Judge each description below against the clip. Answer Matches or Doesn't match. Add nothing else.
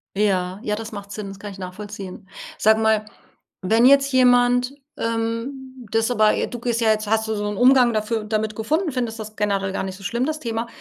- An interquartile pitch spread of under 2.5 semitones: Doesn't match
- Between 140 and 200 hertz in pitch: Doesn't match